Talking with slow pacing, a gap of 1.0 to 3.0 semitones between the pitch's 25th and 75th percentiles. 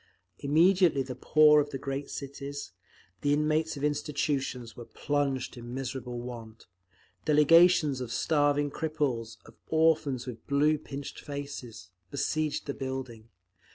Yes: slow, 125 wpm; average, 2.7 semitones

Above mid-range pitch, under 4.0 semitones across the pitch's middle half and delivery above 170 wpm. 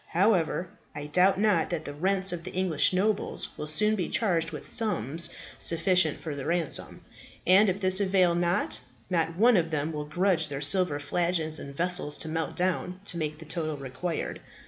No: medium, 170 Hz; average, 3.3 semitones; average, 185 wpm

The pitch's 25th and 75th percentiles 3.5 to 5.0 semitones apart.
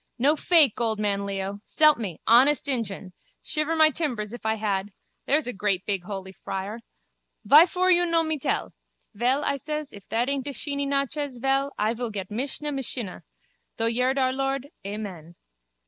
No: wide, 5.6 semitones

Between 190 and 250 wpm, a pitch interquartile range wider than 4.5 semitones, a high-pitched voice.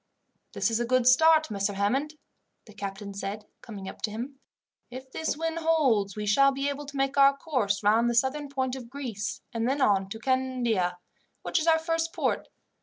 Yes: average, 195 wpm; average, 5.1 semitones; very high, 255 Hz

